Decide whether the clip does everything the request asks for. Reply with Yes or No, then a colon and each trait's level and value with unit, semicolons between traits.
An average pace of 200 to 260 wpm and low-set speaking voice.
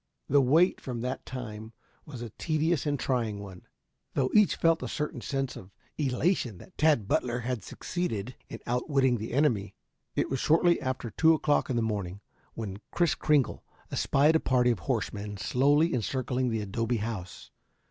No: average, 170 wpm; low, 125 Hz